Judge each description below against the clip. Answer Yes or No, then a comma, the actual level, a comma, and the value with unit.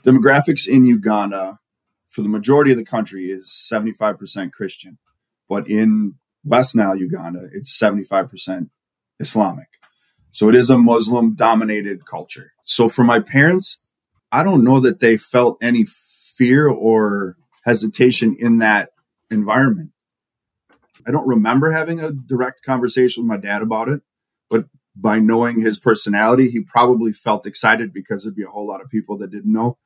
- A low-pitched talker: Yes, low, 115 Hz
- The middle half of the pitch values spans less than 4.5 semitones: Yes, average, 3.1 semitones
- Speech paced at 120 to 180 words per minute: Yes, average, 155 wpm